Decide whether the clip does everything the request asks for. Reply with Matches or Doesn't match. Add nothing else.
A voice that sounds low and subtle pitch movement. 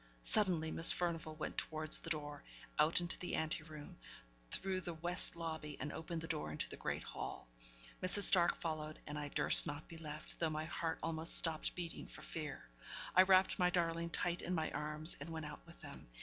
Doesn't match